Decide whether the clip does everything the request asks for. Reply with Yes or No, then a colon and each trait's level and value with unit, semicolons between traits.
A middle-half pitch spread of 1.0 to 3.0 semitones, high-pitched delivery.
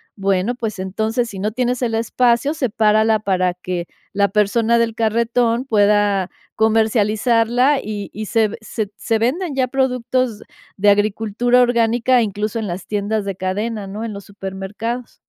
Yes: narrow, 2.6 semitones; high, 220 Hz